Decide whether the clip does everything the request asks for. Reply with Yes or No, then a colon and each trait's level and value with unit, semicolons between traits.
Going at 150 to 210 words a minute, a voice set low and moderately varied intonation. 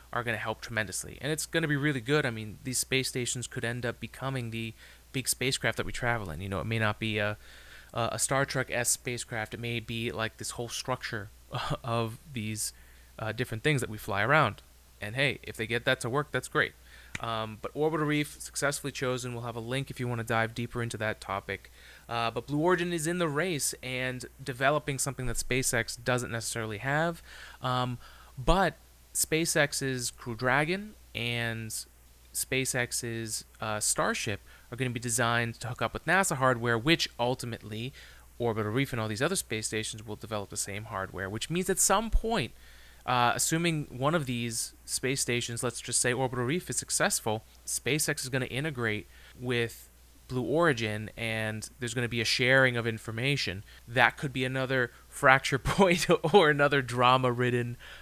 Yes: average, 190 wpm; low, 120 Hz; average, 3.5 semitones